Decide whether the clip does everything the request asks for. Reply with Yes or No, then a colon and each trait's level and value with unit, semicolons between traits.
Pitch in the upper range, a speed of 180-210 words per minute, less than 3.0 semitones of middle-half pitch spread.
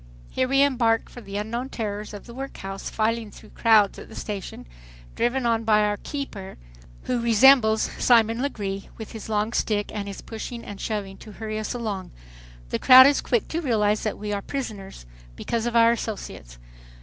Yes: high, 220 Hz; average, 185 wpm; narrow, 2.5 semitones